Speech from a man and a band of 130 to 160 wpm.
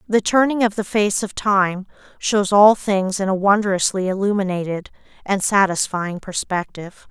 No: female; average, 145 wpm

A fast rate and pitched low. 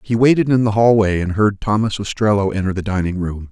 Yes: fast, 220 wpm; low, 105 Hz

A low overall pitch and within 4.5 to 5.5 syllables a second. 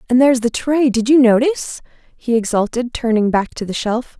No: high, 240 Hz; 5.4 syllables/s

